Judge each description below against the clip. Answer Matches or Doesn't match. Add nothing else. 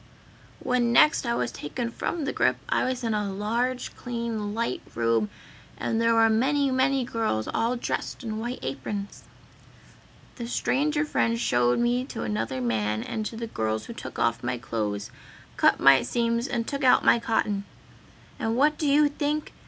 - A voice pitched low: Doesn't match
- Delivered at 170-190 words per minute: Matches